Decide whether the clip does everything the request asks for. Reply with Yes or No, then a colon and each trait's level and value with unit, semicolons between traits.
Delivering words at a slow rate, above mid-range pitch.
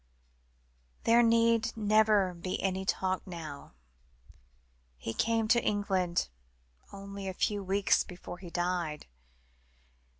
Yes: slow, 105 wpm; high, 195 Hz